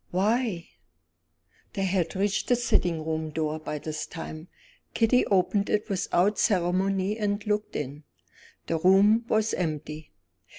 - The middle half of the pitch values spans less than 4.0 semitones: No, average, 4.6 semitones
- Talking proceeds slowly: Yes, slow, 130 wpm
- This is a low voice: No, medium, 185 Hz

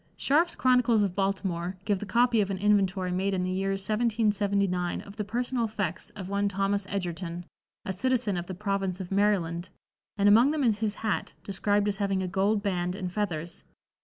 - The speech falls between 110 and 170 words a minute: No, average, 190 wpm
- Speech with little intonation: Yes, narrow, 2.2 semitones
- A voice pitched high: Yes, high, 200 Hz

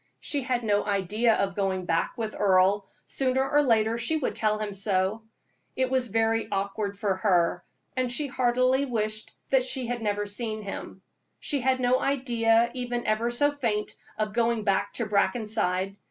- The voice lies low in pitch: No, high, 225 Hz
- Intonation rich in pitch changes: No, average, 3.5 semitones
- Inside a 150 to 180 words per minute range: Yes, average, 170 wpm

